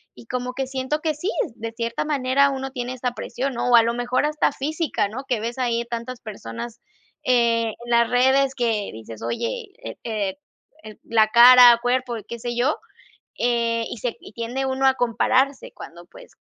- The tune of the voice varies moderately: No, narrow, 2.3 semitones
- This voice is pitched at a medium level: No, high, 245 Hz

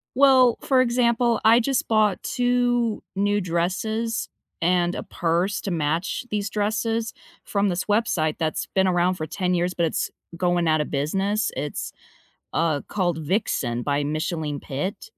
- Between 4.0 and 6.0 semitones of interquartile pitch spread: Yes, average, 5.3 semitones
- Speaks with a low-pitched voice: No, medium, 185 Hz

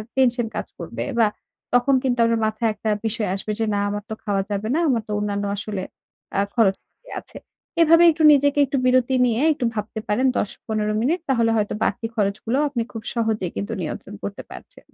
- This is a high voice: Yes, high, 225 Hz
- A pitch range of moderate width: Yes, average, 3.6 semitones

